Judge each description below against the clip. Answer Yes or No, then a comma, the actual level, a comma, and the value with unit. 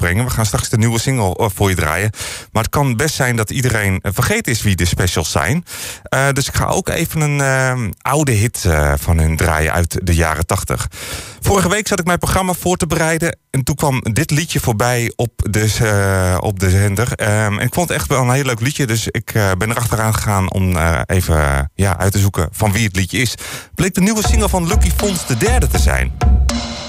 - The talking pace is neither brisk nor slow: No, fast, 220 wpm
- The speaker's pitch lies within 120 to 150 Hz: No, low, 110 Hz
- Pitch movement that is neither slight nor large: No, wide, 6.0 semitones